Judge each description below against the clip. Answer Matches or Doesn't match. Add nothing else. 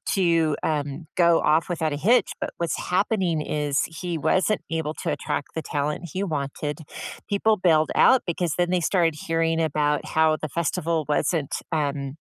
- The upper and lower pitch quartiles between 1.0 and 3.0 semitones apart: Matches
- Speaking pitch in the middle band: Matches